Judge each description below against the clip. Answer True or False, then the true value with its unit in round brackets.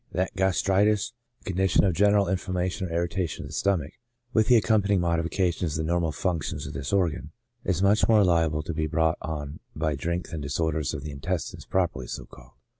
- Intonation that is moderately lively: True (3.4 semitones)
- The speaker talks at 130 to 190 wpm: False (200 wpm)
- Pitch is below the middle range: True (85 Hz)